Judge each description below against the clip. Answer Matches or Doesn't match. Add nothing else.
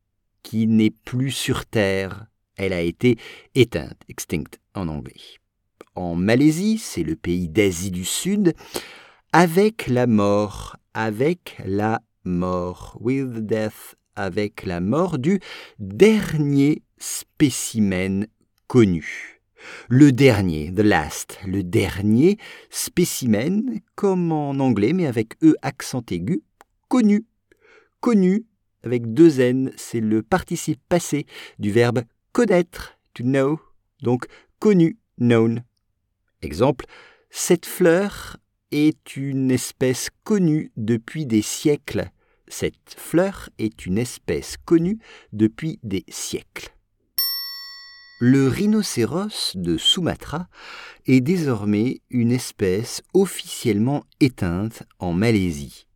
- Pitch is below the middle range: Matches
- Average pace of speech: Doesn't match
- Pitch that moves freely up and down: Matches